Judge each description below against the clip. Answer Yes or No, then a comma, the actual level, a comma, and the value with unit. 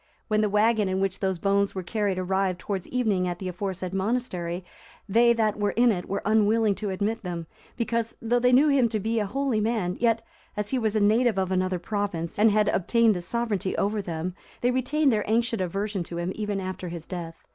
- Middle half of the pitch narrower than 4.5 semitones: Yes, average, 3.4 semitones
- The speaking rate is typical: No, fast, 215 wpm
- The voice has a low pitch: No, high, 205 Hz